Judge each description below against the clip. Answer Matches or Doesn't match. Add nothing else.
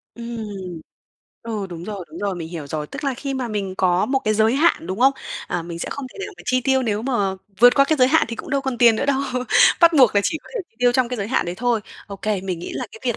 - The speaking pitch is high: Matches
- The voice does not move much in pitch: Doesn't match